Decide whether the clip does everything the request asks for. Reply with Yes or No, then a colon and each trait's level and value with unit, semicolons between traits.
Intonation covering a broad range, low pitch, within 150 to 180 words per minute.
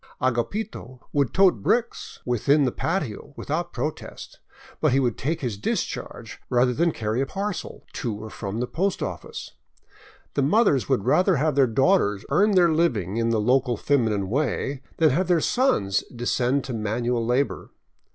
Yes: wide, 5.8 semitones; low, 130 Hz; average, 165 wpm